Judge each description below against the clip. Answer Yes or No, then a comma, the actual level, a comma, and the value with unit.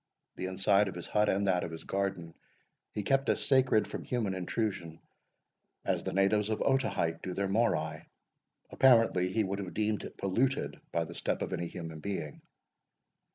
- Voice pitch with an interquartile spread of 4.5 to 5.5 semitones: No, average, 3.6 semitones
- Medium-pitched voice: No, very low, 95 Hz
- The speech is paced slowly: No, average, 175 wpm